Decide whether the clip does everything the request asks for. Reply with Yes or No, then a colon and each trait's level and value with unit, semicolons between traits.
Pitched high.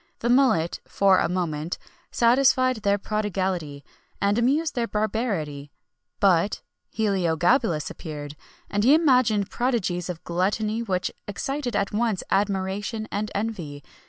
Yes: high, 205 Hz